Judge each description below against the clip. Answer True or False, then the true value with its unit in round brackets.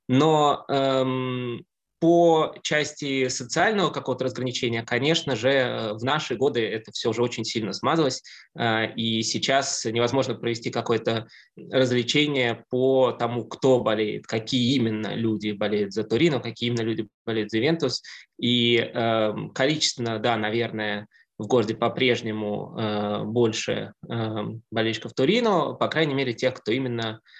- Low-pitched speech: True (120 Hz)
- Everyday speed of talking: True (130 wpm)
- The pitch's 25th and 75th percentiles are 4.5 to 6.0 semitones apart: False (2.8 semitones)